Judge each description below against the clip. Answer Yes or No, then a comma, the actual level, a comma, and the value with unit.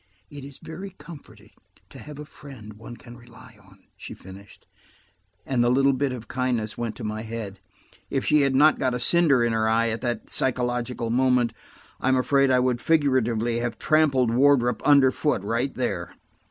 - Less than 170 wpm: No, average, 180 wpm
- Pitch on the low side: Yes, low, 125 Hz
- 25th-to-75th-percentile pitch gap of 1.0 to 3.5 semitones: Yes, average, 3.0 semitones